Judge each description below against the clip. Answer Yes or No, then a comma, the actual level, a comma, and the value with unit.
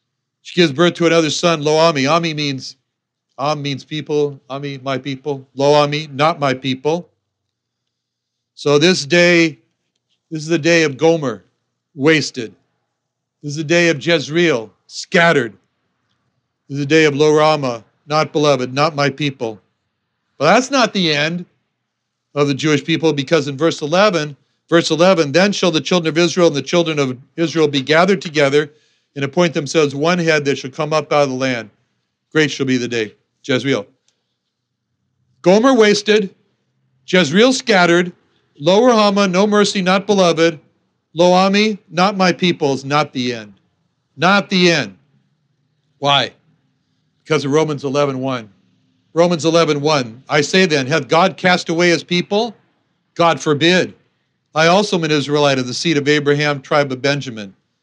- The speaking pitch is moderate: Yes, medium, 155 Hz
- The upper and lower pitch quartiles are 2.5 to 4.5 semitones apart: Yes, average, 3.6 semitones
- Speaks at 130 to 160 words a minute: Yes, average, 155 wpm